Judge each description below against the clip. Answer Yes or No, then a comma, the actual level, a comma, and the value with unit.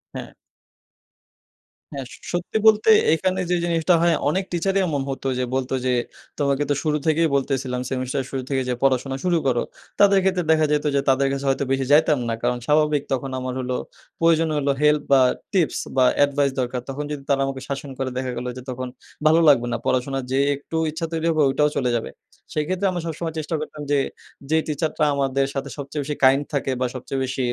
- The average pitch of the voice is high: No, medium, 140 Hz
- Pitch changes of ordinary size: Yes, average, 3.2 semitones